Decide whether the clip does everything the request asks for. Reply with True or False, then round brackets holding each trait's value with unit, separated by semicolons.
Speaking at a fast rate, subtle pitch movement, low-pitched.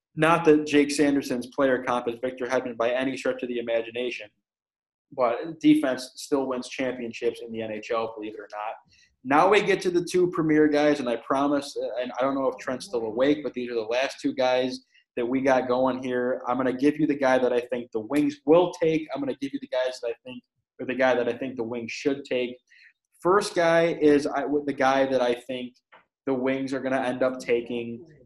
False (230 wpm; 3.0 semitones; 130 Hz)